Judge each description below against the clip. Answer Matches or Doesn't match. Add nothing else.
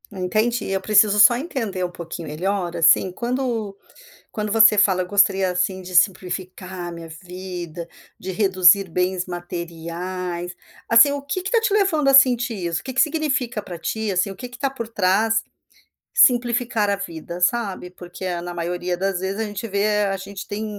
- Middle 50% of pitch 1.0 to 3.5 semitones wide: Doesn't match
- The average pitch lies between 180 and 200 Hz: Matches